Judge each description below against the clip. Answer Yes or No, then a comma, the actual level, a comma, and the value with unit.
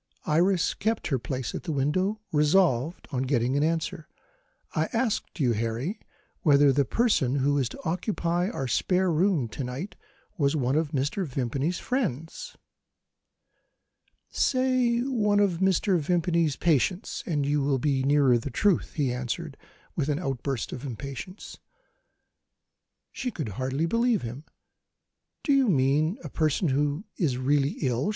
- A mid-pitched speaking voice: Yes, medium, 150 Hz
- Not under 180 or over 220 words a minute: No, average, 145 wpm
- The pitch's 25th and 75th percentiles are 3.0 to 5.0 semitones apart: No, wide, 5.6 semitones